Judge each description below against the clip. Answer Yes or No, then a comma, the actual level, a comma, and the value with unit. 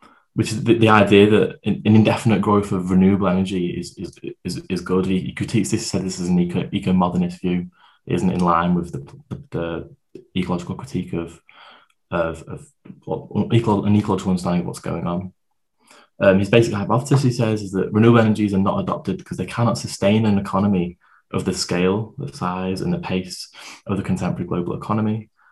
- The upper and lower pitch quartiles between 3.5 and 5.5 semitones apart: No, average, 3.1 semitones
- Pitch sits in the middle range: No, very low, 95 Hz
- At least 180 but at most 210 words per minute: Yes, average, 185 wpm